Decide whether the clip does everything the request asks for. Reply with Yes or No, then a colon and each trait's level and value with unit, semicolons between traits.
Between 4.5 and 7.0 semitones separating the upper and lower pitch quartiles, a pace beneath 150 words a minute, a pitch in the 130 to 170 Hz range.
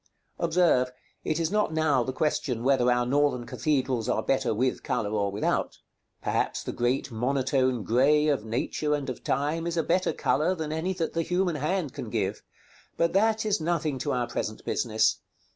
No: average, 4.8 semitones; average, 180 wpm; medium, 140 Hz